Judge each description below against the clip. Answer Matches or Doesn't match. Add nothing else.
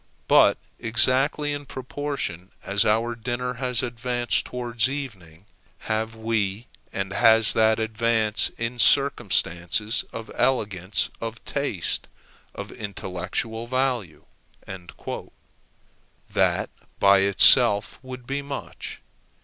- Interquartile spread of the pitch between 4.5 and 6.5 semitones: Doesn't match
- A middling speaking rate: Doesn't match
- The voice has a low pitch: Matches